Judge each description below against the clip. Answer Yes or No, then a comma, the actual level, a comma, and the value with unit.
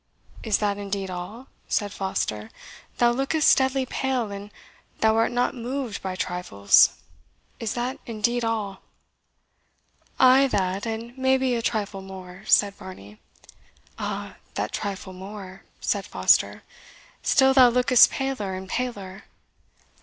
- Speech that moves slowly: Yes, slow, 125 wpm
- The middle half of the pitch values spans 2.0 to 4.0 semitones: No, average, 4.7 semitones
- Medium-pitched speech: No, high, 215 Hz